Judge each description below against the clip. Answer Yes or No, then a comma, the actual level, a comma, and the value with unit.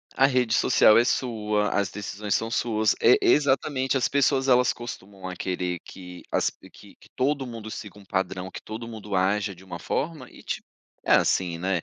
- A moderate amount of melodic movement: Yes, average, 4.9 semitones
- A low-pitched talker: Yes, low, 110 Hz